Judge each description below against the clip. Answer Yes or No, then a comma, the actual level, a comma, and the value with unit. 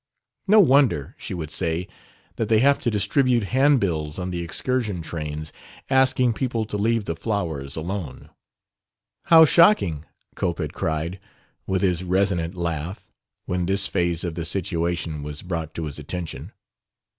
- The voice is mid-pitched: No, very low, 90 Hz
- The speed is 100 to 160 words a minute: Yes, average, 145 wpm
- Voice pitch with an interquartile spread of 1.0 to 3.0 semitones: No, average, 5.3 semitones